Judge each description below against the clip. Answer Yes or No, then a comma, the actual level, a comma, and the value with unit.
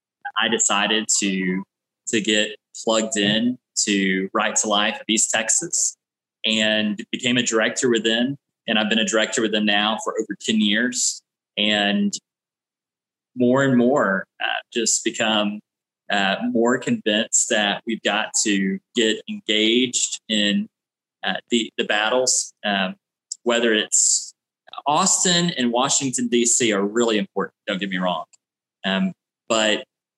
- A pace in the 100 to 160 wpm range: Yes, slow, 135 wpm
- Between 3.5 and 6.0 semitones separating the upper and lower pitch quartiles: No, average, 2.8 semitones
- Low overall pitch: Yes, low, 110 Hz